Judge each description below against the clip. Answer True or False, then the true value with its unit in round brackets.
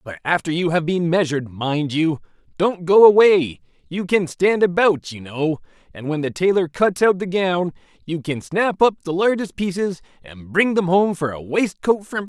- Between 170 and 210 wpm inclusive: True (200 wpm)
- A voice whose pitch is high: False (170 Hz)